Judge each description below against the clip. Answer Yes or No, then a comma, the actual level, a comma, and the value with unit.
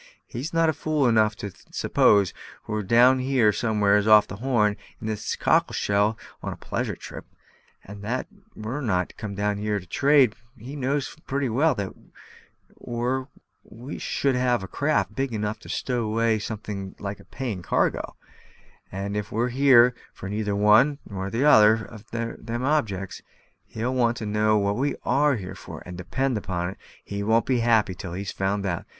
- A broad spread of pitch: No, average, 3.8 semitones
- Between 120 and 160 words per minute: No, average, 175 wpm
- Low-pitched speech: Yes, low, 110 Hz